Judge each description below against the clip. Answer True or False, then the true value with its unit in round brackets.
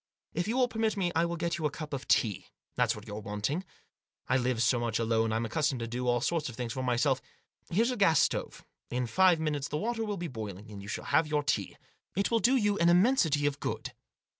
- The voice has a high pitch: False (145 Hz)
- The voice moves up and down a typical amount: False (7.1 semitones)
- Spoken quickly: True (240 wpm)